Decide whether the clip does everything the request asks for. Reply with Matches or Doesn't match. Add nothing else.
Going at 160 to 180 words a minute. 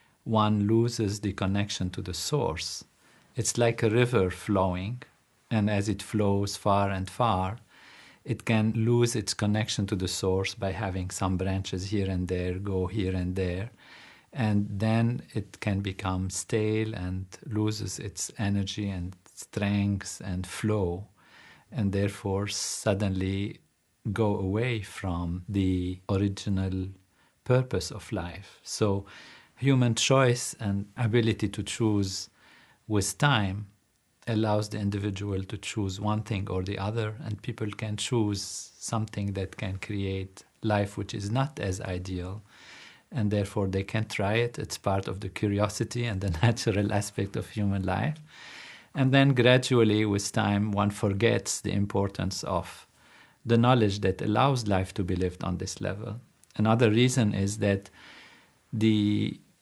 Doesn't match